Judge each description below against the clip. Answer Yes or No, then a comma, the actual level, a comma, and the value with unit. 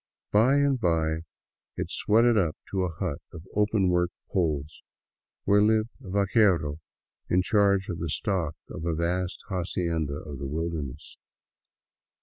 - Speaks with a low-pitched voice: Yes, very low, 90 Hz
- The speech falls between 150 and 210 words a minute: No, average, 140 wpm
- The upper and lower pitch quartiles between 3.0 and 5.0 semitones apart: Yes, average, 4.1 semitones